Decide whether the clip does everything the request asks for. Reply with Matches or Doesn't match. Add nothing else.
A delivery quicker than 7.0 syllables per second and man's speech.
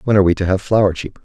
Matches